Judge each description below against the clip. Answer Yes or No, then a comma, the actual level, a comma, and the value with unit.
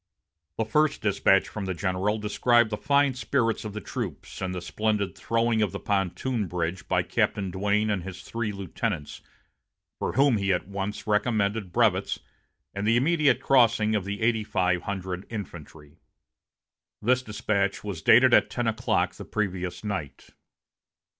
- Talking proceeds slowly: No, average, 155 wpm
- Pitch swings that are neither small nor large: Yes, average, 3.3 semitones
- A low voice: Yes, low, 105 Hz